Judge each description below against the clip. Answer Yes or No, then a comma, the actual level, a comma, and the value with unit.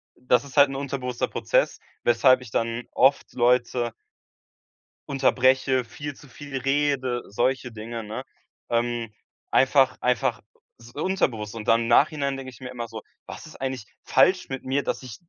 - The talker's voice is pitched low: Yes, low, 130 Hz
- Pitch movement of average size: No, narrow, 2.3 semitones